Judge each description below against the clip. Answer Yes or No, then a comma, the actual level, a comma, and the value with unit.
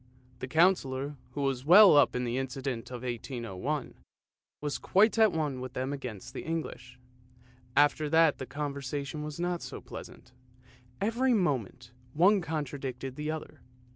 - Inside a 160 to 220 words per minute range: No, average, 145 wpm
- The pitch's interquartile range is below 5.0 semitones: Yes, average, 4.0 semitones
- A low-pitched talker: No, medium, 145 Hz